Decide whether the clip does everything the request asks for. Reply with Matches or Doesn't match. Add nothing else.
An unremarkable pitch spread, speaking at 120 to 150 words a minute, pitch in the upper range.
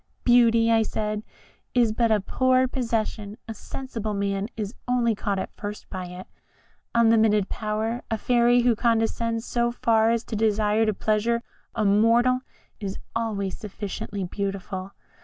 Doesn't match